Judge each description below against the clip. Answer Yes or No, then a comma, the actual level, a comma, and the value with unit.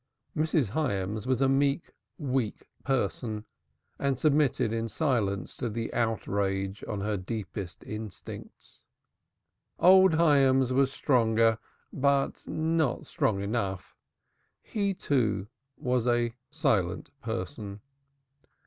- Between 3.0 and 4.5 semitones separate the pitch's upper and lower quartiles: No, average, 4.9 semitones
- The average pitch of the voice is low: Yes, low, 120 Hz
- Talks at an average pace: No, slow, 105 wpm